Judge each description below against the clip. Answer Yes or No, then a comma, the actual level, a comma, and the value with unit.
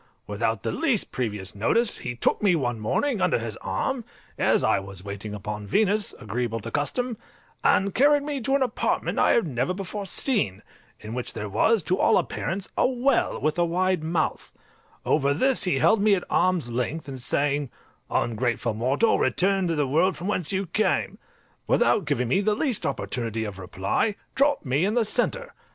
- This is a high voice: No, medium, 165 Hz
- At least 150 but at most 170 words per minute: No, average, 185 wpm